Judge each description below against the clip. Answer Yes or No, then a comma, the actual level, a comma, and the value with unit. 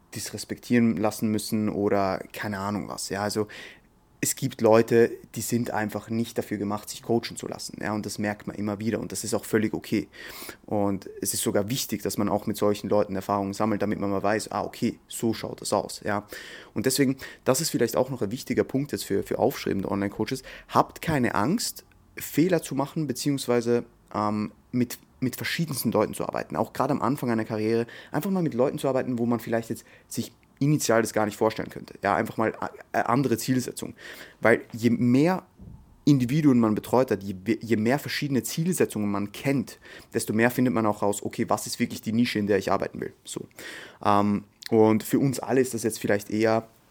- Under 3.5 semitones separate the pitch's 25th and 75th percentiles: Yes, average, 3.0 semitones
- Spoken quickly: Yes, fast, 200 wpm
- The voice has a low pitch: Yes, low, 115 Hz